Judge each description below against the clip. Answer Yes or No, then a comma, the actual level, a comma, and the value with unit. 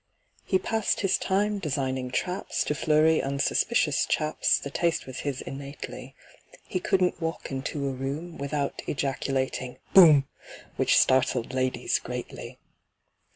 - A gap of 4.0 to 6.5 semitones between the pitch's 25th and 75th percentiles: Yes, average, 4.3 semitones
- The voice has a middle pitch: Yes, medium, 145 Hz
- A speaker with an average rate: No, slow, 125 wpm